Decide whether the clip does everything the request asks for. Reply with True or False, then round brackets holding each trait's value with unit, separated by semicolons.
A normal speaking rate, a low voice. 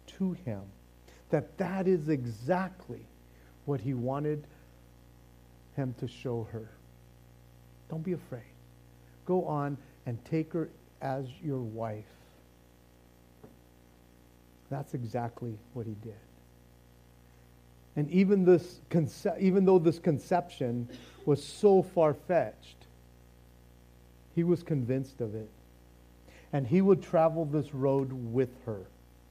False (110 wpm; 115 Hz)